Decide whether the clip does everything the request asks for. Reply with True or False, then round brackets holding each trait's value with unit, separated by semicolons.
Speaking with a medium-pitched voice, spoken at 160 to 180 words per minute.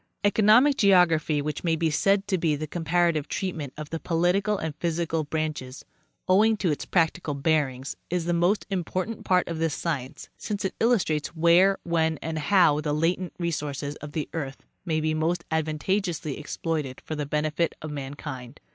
True (160 Hz; 165 wpm)